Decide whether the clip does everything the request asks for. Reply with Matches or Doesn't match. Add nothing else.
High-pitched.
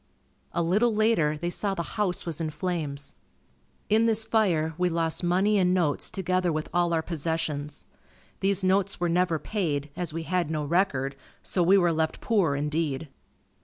Doesn't match